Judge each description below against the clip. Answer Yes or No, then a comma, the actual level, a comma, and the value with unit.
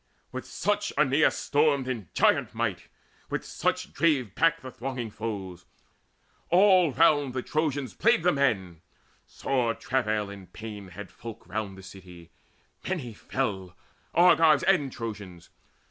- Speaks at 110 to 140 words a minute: Yes, slow, 135 wpm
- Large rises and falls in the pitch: Yes, wide, 6.9 semitones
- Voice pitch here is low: Yes, low, 125 Hz